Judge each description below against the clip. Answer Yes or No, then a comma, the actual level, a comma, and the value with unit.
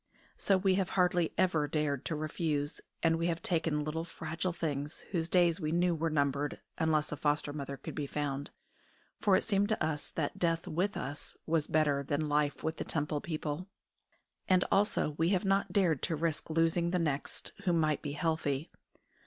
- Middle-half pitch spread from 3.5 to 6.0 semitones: No, average, 2.8 semitones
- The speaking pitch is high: No, medium, 160 Hz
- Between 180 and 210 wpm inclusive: Yes, average, 185 wpm